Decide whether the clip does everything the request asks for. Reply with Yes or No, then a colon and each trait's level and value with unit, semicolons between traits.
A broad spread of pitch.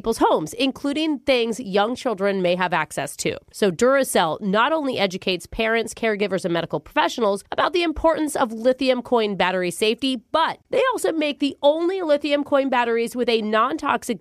Yes: wide, 5.8 semitones